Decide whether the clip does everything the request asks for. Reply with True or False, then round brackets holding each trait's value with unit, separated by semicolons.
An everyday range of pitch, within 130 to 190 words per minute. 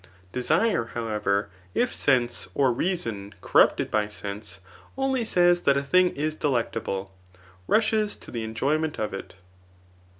False (8.7 semitones; 135 wpm)